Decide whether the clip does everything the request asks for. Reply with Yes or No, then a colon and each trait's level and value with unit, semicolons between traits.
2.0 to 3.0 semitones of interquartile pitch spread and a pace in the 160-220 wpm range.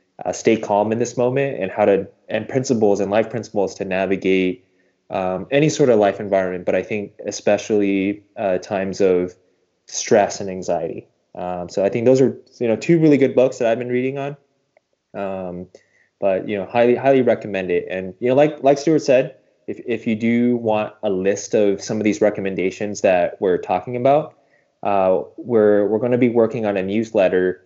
No: average, 4.4 semitones; average, 195 wpm